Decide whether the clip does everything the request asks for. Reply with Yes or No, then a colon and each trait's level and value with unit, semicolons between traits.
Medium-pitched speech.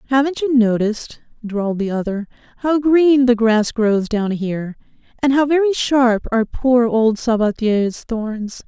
No: high, 235 Hz